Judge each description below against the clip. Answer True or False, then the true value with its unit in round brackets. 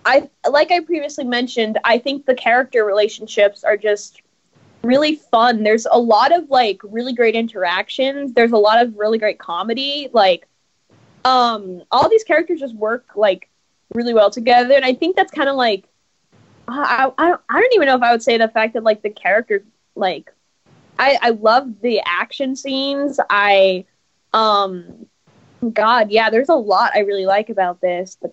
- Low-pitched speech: False (235 Hz)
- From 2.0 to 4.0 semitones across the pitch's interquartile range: False (4.4 semitones)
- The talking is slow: False (175 wpm)